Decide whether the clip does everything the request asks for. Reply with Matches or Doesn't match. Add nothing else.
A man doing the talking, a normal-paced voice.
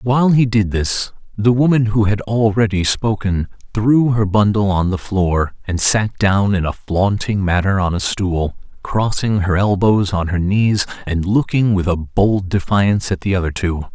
Matches